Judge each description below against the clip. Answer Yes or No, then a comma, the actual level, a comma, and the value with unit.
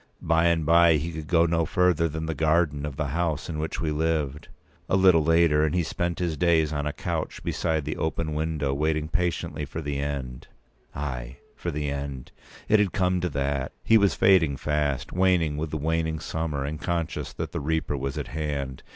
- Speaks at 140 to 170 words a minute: No, fast, 205 wpm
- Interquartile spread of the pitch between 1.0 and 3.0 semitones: Yes, narrow, 2.5 semitones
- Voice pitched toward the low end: Yes, very low, 80 Hz